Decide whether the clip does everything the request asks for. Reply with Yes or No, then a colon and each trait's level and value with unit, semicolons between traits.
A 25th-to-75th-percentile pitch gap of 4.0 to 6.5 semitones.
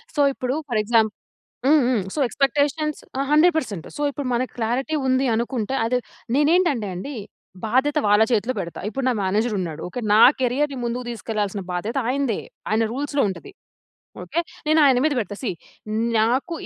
Yes: average, 4.7 semitones